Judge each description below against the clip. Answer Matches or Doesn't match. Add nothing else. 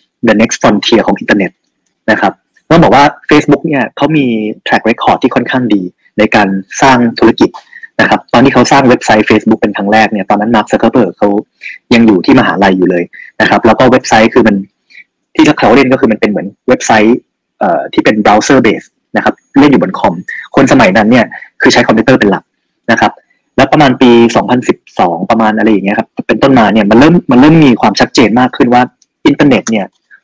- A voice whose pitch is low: Matches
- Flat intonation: Doesn't match